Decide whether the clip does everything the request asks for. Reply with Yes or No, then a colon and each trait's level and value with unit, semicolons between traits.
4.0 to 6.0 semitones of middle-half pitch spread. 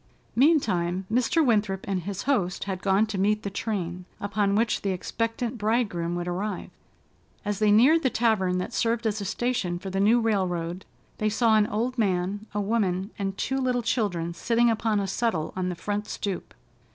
No: average, 3.5 semitones